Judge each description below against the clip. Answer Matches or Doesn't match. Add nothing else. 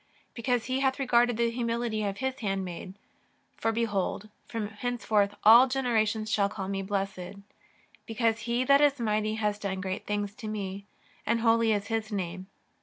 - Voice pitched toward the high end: Matches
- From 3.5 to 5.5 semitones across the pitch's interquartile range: Doesn't match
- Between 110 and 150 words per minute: Doesn't match